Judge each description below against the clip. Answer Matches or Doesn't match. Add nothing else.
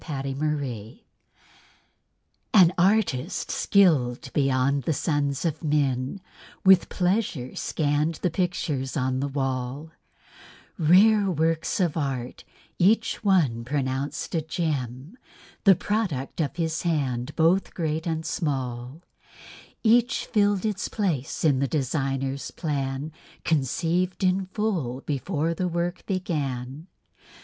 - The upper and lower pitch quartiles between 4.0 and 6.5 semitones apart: Matches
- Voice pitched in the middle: Matches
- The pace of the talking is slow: Matches